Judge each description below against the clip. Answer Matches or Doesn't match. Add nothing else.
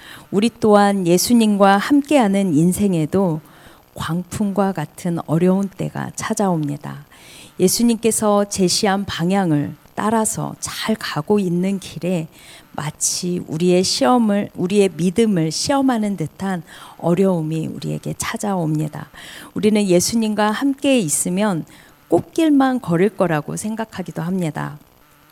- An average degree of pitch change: Matches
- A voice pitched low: Doesn't match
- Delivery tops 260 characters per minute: Matches